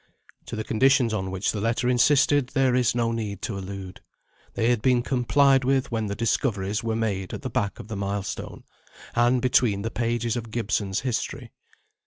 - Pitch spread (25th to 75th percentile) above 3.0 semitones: Yes, average, 3.7 semitones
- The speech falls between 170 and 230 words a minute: Yes, average, 185 wpm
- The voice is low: Yes, low, 115 Hz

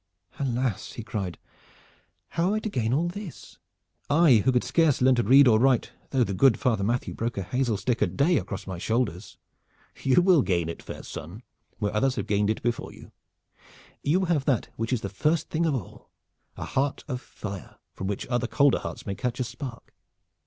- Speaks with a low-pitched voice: Yes, low, 125 Hz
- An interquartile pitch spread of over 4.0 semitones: Yes, average, 4.8 semitones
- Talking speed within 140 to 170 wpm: No, average, 200 wpm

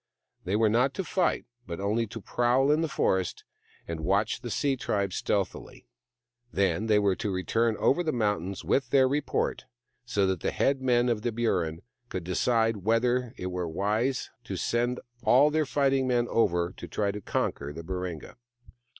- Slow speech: No, average, 175 wpm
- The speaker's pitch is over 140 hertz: No, low, 110 Hz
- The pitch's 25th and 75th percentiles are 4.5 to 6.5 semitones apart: Yes, average, 4.9 semitones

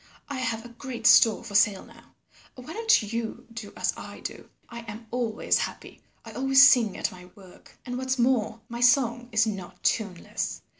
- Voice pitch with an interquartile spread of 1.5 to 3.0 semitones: Yes, narrow, 2.6 semitones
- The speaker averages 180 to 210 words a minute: Yes, average, 185 wpm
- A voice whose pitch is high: Yes, high, 235 Hz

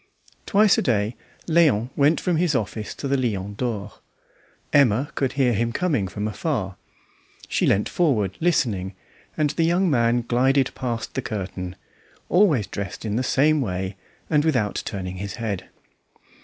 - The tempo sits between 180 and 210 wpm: No, average, 155 wpm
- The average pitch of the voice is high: No, low, 120 Hz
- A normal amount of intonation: No, wide, 6.2 semitones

